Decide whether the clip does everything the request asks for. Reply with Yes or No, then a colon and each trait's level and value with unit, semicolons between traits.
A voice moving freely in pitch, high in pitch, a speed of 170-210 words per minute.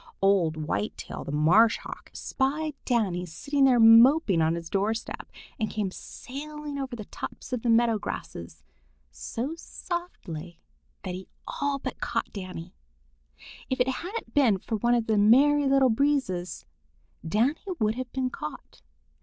No: wide, 6.6 semitones; high, 230 Hz; average, 150 wpm